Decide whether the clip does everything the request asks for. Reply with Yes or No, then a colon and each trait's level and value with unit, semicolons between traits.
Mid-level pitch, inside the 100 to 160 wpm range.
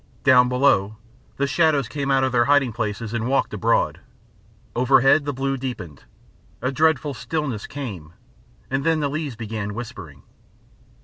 No: low, 130 Hz; average, 145 wpm